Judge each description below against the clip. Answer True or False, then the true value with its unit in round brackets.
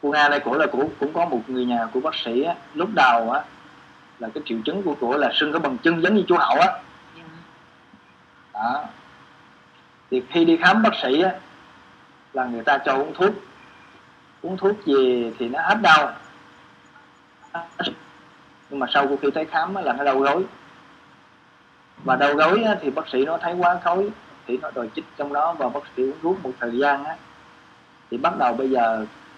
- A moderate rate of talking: True (195 wpm)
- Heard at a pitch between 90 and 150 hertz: True (135 Hz)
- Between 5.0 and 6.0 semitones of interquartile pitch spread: True (5.6 semitones)